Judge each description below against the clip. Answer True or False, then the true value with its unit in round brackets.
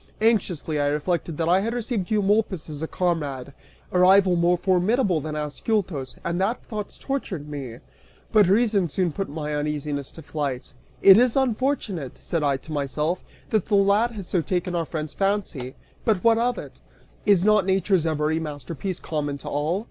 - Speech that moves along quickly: False (175 wpm)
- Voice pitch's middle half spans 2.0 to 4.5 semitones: False (5.3 semitones)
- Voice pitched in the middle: True (175 Hz)